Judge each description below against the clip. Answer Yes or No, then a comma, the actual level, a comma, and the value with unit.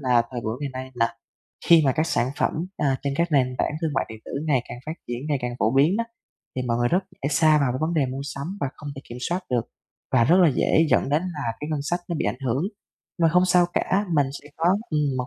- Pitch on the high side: No, medium, 140 Hz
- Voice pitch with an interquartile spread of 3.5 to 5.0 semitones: Yes, average, 4.3 semitones